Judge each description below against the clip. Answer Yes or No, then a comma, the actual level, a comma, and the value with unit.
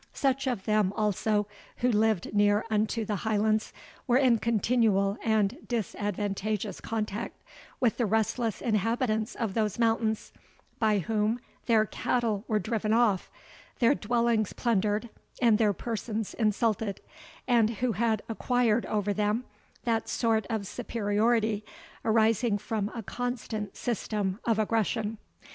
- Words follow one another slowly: Yes, slow, 125 wpm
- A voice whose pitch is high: Yes, high, 220 Hz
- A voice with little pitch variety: Yes, narrow, 1.8 semitones